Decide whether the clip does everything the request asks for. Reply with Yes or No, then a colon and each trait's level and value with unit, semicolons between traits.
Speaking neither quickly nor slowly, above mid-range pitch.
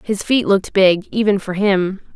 Yes: average, 195 wpm; high, 200 Hz